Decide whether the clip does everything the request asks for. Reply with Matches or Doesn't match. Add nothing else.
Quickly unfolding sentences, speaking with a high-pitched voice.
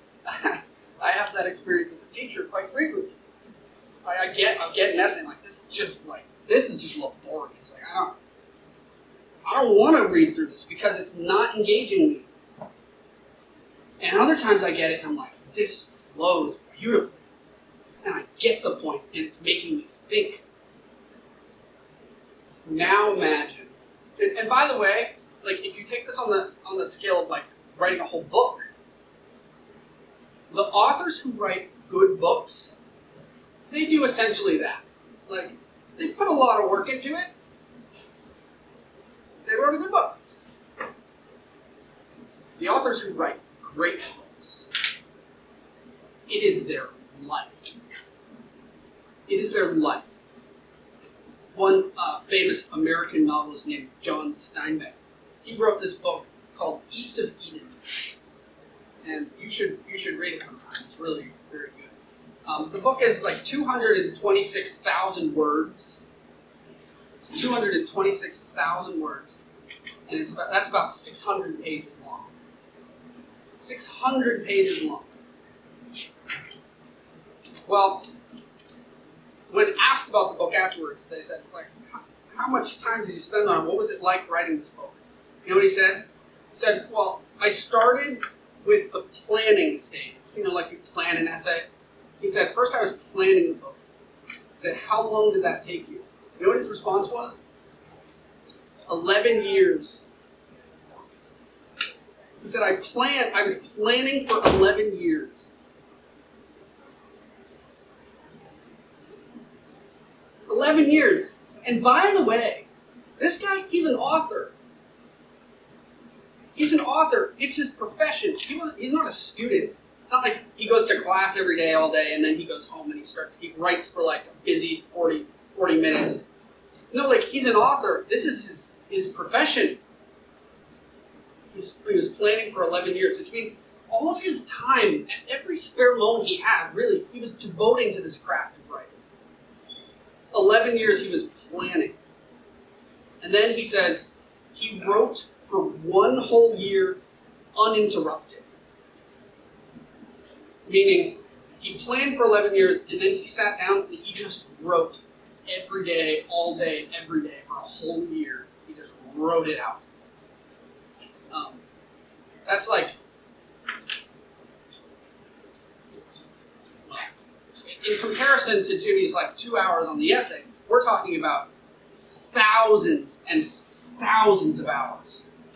Doesn't match